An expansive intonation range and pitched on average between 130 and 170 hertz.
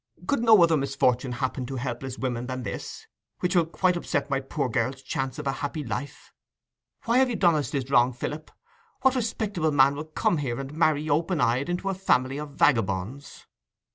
No: average, 4.5 semitones; medium, 140 Hz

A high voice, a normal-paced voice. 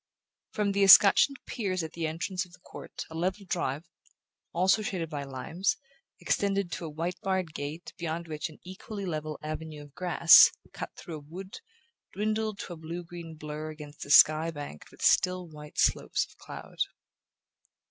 No: medium, 170 Hz; average, 170 wpm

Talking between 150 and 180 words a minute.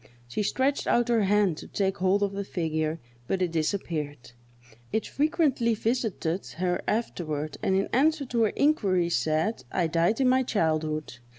Yes: average, 170 wpm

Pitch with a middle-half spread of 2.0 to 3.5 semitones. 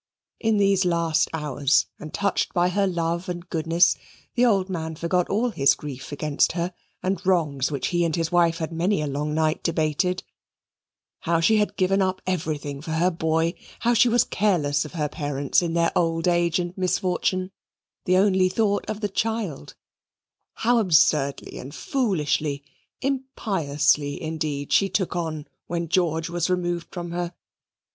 Yes: average, 3.2 semitones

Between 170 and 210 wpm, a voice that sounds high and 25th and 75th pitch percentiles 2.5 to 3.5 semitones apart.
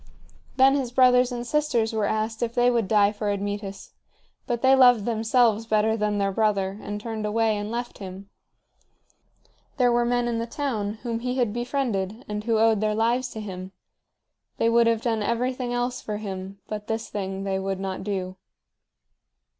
Yes: average, 180 wpm; high, 225 Hz; average, 2.8 semitones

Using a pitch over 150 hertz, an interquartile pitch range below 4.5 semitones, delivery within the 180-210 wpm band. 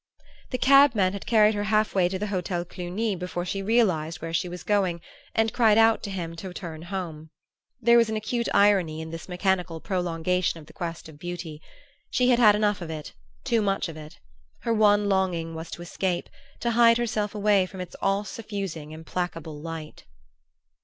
Yes: medium, 185 Hz; average, 4.1 semitones; average, 190 wpm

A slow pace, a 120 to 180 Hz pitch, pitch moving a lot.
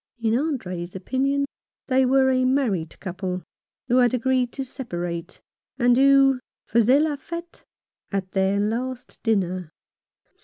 No: slow, 125 wpm; high, 245 Hz; wide, 5.7 semitones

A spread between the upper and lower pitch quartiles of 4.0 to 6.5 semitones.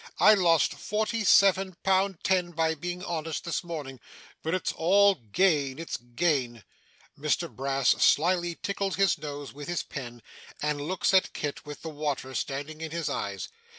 Yes: average, 4.5 semitones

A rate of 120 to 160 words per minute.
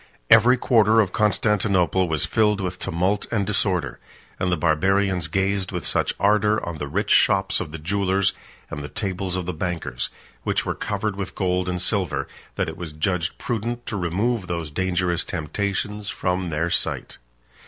No: average, 175 wpm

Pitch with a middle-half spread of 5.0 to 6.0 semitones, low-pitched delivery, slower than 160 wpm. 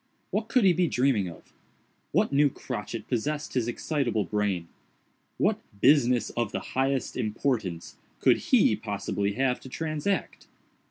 Yes: wide, 5.5 semitones; low, 125 Hz; average, 140 wpm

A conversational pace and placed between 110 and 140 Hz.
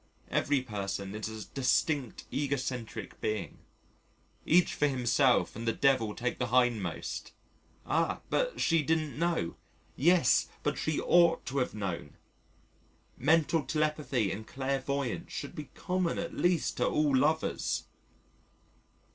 No: slow, 125 wpm; low, 135 Hz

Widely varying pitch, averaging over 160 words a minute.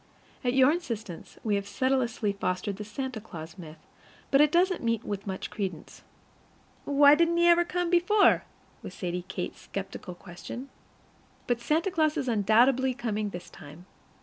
No: wide, 6.7 semitones; average, 155 wpm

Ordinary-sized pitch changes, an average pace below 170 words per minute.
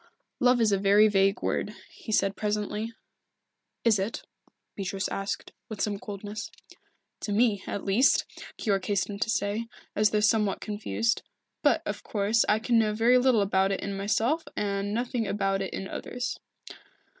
No: narrow, 2.2 semitones; average, 160 wpm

